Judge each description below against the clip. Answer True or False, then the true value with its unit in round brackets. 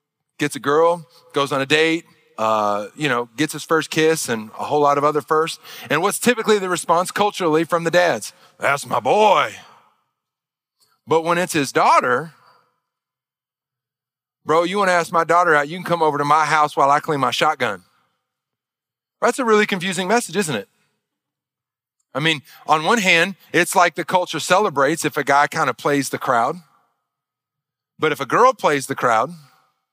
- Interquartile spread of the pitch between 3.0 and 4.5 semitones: True (3.8 semitones)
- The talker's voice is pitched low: False (155 Hz)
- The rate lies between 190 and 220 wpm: False (180 wpm)